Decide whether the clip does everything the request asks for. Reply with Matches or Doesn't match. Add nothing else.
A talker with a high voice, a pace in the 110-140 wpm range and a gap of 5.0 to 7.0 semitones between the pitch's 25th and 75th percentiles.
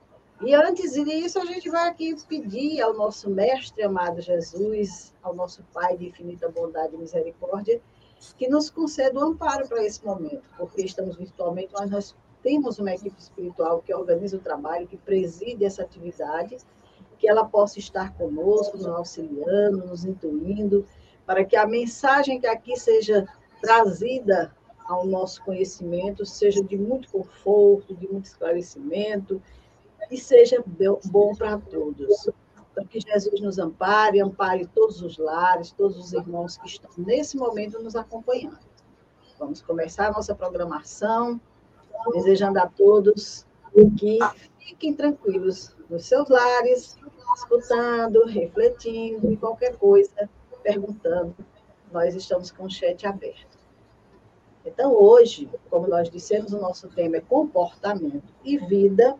Matches